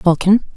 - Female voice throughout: Yes, female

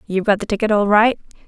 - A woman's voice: Yes, female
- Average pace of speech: No, fast, 245 wpm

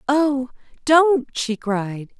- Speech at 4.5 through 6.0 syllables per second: No, 2.5 syllables/s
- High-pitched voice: Yes, very high, 260 Hz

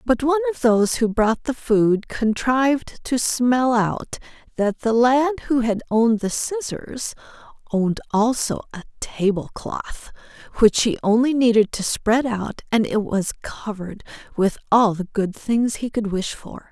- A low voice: No, high, 235 Hz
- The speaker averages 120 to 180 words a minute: Yes, average, 160 wpm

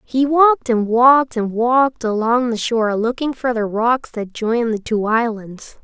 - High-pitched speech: Yes, high, 235 Hz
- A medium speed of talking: Yes, average, 185 wpm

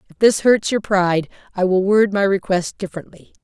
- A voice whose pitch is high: Yes, high, 195 Hz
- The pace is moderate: Yes, average, 190 wpm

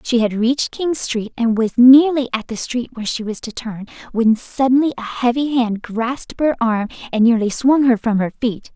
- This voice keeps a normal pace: No, fast, 210 wpm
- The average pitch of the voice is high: Yes, high, 240 Hz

